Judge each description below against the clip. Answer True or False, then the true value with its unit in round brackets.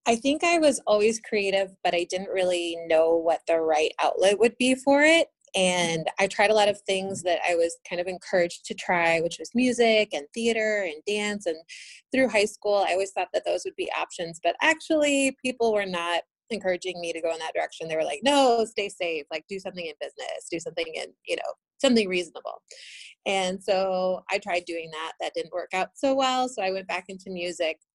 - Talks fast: True (215 wpm)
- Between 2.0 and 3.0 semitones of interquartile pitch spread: False (5.2 semitones)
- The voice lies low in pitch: False (195 Hz)